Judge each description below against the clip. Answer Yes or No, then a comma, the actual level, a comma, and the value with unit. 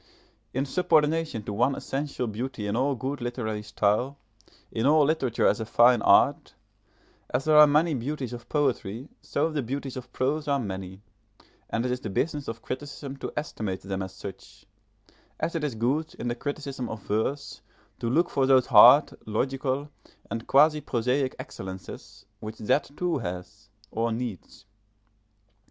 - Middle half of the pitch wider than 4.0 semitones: Yes, average, 4.5 semitones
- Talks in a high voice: No, low, 130 Hz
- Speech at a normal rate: Yes, average, 160 wpm